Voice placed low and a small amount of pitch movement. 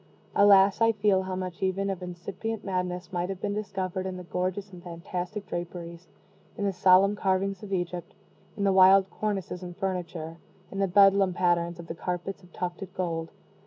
No: medium, 185 Hz; narrow, 1.8 semitones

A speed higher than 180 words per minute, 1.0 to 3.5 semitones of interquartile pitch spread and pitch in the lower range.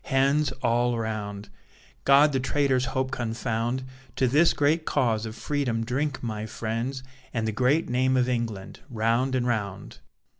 No: average, 150 wpm; average, 2.9 semitones; low, 125 Hz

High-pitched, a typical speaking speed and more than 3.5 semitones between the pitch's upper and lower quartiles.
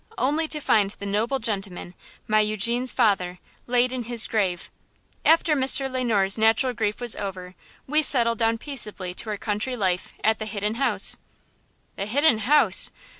Yes: high, 225 Hz; average, 165 wpm; average, 3.9 semitones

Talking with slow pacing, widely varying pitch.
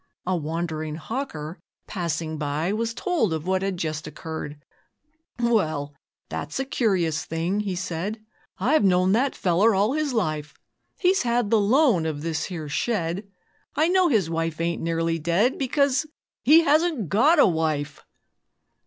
No: average, 150 wpm; wide, 6.8 semitones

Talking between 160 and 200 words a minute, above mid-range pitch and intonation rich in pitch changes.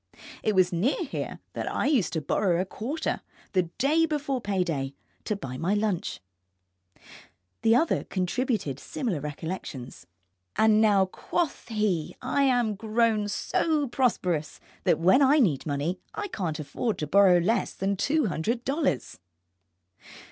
No: average, 145 wpm; high, 205 Hz; wide, 6.6 semitones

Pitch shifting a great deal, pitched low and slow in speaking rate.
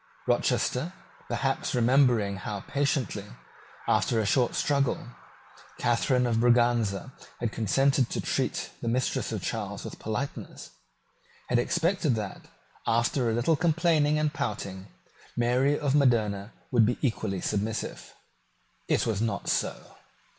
No: average, 4.0 semitones; low, 120 Hz; slow, 125 wpm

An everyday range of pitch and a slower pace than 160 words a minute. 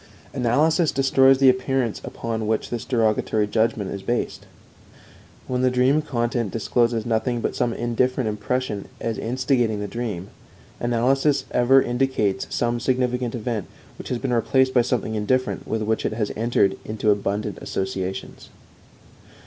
Yes: average, 3.0 semitones; average, 140 wpm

